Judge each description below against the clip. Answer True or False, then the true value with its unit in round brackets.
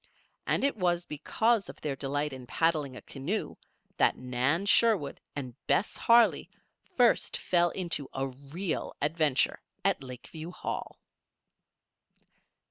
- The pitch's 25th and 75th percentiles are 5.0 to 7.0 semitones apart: True (5.5 semitones)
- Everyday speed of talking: False (125 wpm)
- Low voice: False (155 Hz)